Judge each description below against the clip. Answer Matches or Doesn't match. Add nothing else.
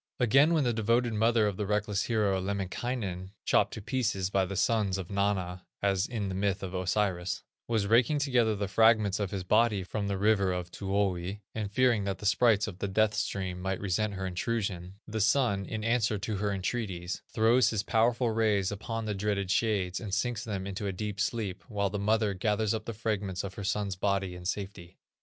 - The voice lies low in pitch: Matches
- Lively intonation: Doesn't match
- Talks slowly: Doesn't match